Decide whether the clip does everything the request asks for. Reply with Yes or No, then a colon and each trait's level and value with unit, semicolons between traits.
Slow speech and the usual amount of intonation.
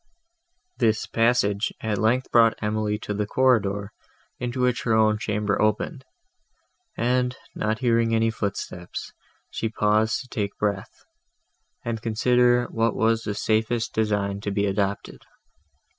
No: slow, 130 wpm; narrow, 2.2 semitones